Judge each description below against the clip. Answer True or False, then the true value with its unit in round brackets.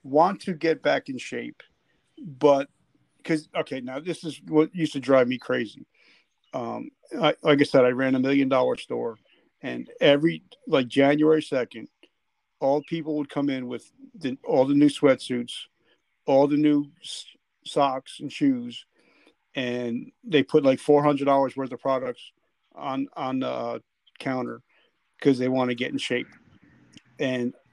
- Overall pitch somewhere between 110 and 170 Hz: True (140 Hz)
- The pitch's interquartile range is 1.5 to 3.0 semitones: True (2.7 semitones)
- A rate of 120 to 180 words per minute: True (160 wpm)